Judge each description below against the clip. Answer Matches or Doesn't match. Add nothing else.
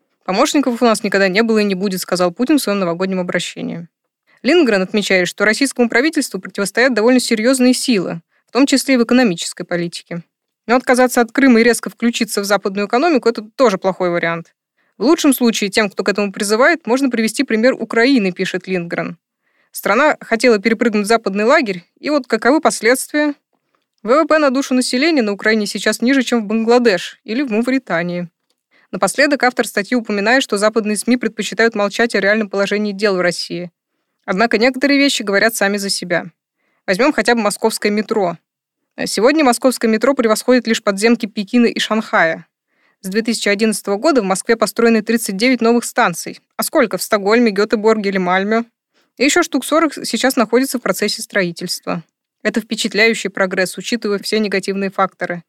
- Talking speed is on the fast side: Matches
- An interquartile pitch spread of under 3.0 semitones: Doesn't match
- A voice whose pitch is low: Doesn't match